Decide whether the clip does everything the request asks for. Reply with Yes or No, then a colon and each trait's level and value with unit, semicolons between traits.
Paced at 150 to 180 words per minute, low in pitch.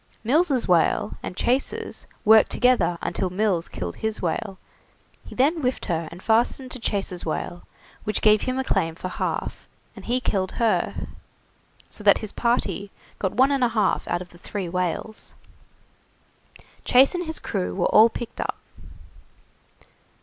No: average, 155 wpm; high, 215 Hz